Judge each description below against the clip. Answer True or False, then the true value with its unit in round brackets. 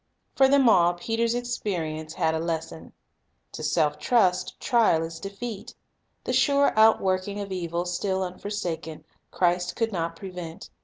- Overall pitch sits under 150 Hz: False (185 Hz)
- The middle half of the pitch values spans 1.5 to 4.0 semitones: False (4.8 semitones)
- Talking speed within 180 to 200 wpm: False (140 wpm)